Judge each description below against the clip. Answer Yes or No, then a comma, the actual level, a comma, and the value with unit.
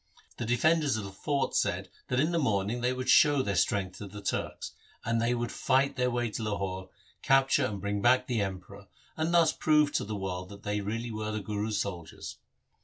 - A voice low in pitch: Yes, low, 110 Hz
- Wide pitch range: No, average, 4.5 semitones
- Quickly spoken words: Yes, fast, 210 wpm